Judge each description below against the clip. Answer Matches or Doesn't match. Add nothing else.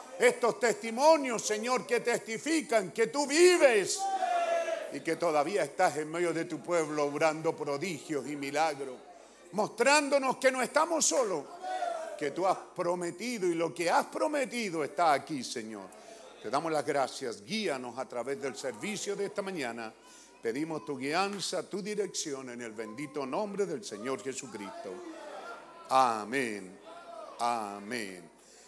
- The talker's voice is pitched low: Doesn't match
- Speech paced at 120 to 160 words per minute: Matches